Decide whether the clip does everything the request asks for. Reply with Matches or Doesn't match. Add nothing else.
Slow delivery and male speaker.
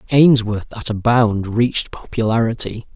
Matches